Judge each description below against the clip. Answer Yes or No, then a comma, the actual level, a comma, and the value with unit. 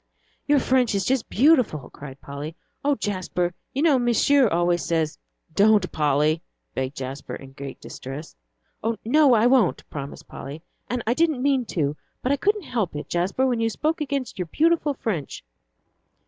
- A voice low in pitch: No, high, 210 Hz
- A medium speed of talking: Yes, average, 165 wpm